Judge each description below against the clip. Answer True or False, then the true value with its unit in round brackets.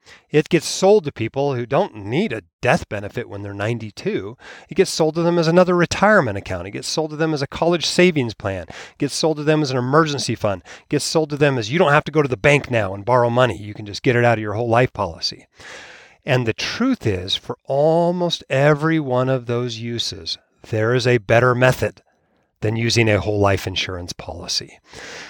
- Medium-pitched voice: False (125 Hz)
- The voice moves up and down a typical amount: False (6.3 semitones)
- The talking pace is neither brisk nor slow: False (225 wpm)